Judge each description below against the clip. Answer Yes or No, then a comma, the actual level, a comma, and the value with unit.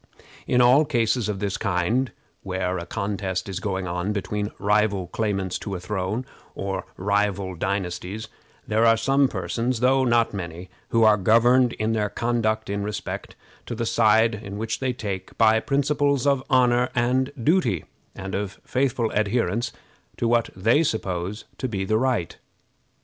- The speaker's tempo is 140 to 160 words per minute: Yes, average, 155 wpm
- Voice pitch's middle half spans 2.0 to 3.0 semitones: No, average, 3.8 semitones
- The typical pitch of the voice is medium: No, low, 110 Hz